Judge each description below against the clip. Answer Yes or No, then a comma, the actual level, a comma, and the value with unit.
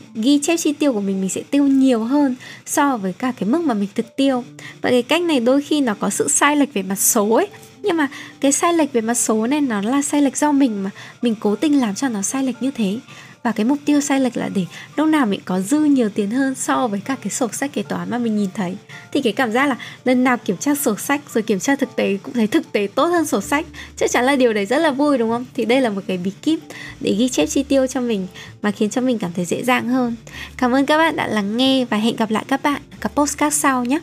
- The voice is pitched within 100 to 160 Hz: No, very high, 255 Hz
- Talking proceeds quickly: Yes, fast, 290 wpm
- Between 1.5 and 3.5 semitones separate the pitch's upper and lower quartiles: No, average, 4.9 semitones